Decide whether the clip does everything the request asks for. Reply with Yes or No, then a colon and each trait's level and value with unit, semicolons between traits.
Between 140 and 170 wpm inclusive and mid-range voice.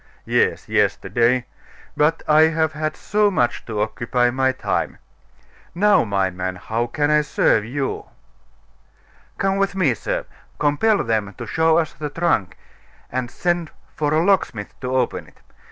Yes: average, 150 wpm; medium, 145 Hz